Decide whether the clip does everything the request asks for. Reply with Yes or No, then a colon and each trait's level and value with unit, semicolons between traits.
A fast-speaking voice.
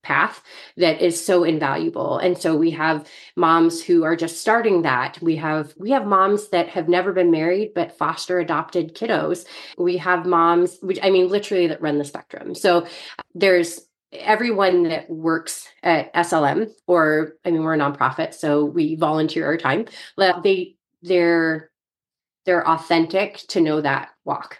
No: average, 160 wpm